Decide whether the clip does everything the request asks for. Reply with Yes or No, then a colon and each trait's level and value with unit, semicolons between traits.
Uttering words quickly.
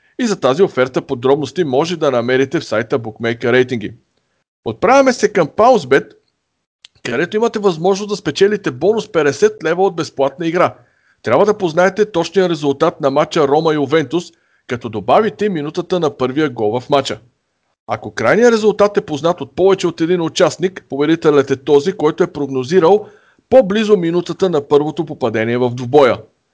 No: average, 155 wpm